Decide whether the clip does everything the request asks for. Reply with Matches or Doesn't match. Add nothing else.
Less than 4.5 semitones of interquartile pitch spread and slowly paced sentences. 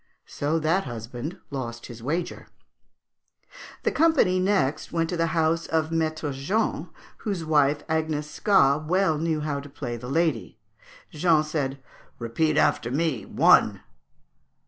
Matches